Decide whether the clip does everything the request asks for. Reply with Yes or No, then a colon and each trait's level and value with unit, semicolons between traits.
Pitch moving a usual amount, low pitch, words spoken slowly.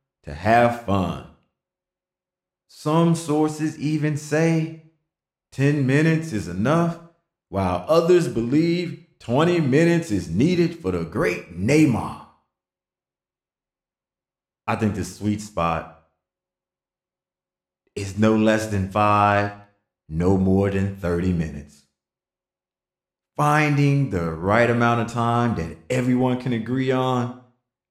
No: wide, 7.9 semitones; low, 120 Hz; slow, 105 wpm